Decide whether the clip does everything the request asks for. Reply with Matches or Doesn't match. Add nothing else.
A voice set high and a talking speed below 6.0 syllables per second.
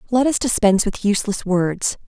Matches